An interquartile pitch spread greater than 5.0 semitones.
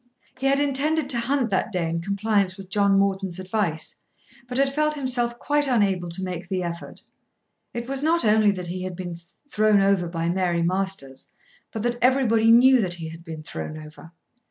Yes: wide, 5.6 semitones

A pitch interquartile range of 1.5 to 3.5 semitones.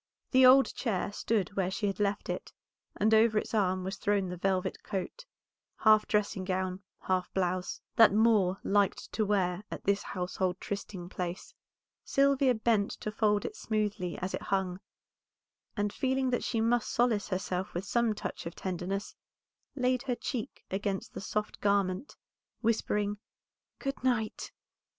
Yes: average, 3.2 semitones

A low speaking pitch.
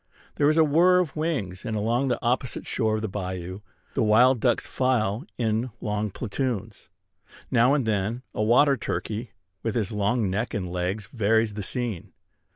Yes: low, 110 Hz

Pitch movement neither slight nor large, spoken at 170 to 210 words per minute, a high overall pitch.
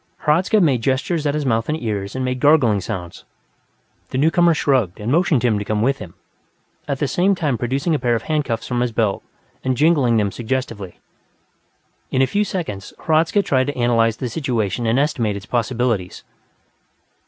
No: average, 4.9 semitones; average, 180 wpm; low, 125 Hz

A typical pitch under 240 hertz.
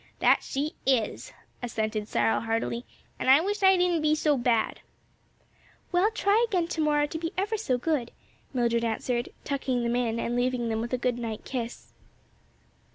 No: very high, 255 Hz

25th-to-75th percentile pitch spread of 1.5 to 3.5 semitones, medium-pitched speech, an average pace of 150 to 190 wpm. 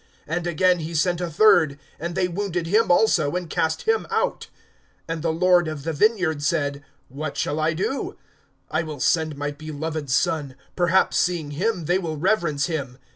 Yes: average, 2.9 semitones; medium, 165 Hz; average, 180 wpm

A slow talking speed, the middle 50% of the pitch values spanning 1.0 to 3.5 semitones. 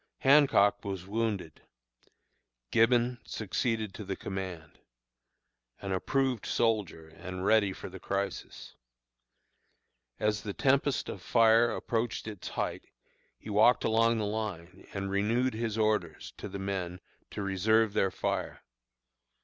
Yes: slow, 125 wpm; average, 2.9 semitones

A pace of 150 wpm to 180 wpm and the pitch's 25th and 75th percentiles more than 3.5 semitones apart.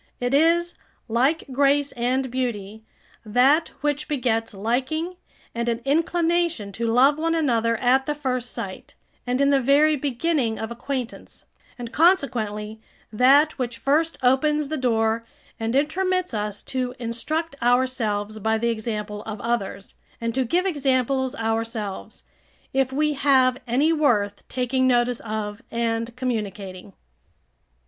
No: slow, 135 wpm; average, 4.0 semitones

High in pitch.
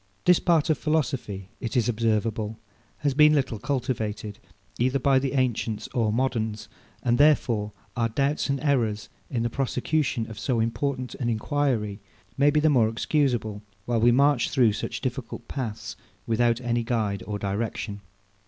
No: low, 120 Hz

